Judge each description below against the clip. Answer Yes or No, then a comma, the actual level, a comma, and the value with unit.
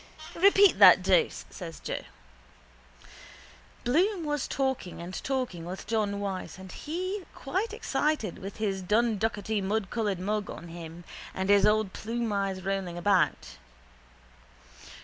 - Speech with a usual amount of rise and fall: No, wide, 5.9 semitones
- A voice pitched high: Yes, high, 210 Hz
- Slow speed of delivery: Yes, slow, 115 wpm